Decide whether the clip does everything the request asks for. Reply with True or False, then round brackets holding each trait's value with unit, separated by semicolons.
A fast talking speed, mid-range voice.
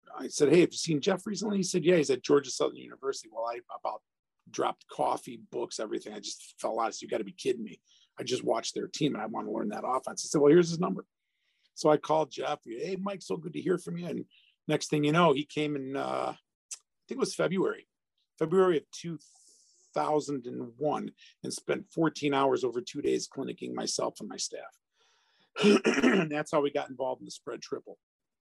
True (220 wpm; 160 Hz)